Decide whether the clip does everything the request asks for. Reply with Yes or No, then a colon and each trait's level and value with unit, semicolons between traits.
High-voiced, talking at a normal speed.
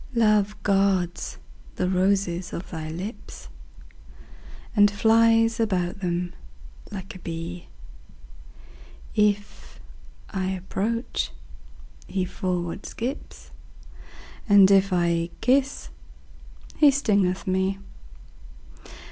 No: high, 195 Hz; slow, 85 wpm